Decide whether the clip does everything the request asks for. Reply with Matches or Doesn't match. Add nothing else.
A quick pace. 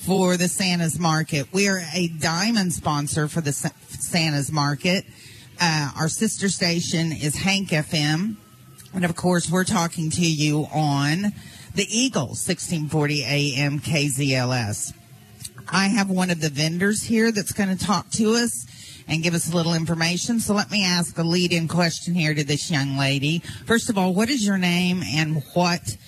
Doesn't match